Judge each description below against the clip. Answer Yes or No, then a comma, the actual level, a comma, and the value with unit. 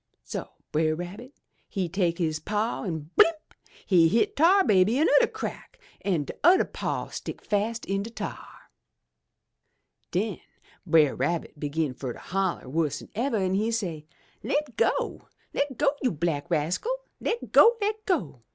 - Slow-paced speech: No, average, 150 wpm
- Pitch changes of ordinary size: No, wide, 6.5 semitones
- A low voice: No, high, 190 Hz